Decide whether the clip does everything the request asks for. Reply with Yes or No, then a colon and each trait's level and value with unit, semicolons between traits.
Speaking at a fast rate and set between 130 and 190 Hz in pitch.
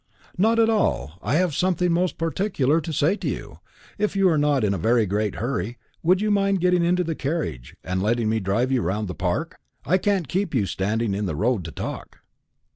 Yes: fast, 215 wpm; medium, 140 Hz